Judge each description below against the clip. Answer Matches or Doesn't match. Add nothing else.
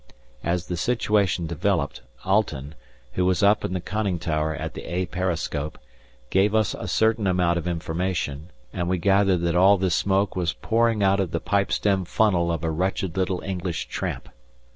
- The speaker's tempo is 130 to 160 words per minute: Doesn't match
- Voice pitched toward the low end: Matches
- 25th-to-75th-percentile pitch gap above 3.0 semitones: Doesn't match